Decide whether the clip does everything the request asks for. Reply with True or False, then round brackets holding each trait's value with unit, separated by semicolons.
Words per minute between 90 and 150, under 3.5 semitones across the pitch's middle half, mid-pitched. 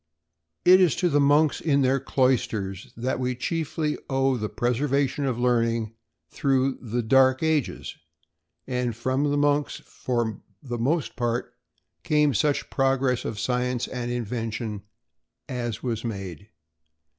False (135 wpm; 3.1 semitones; 125 Hz)